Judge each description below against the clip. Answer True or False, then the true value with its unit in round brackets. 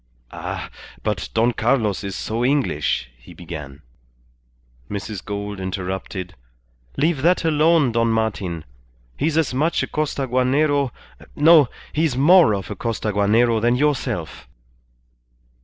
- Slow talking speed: True (115 wpm)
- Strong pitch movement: True (6.4 semitones)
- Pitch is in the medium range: False (120 Hz)